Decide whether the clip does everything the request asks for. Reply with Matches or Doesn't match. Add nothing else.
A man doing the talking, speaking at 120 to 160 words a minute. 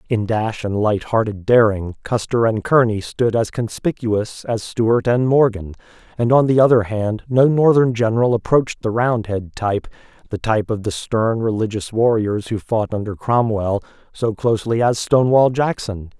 Matches